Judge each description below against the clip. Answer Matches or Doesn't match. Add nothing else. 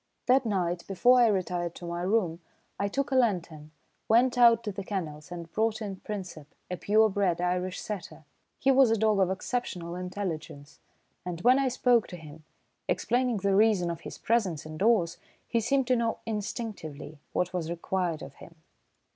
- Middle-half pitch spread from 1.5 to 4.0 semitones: Doesn't match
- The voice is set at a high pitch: Matches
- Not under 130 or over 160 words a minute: Doesn't match